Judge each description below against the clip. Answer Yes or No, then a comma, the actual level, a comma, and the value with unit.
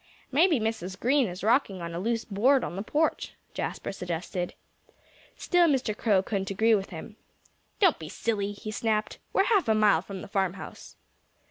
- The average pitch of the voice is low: No, high, 215 Hz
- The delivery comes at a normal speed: Yes, average, 170 wpm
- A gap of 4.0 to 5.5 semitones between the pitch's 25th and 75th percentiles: Yes, average, 4.3 semitones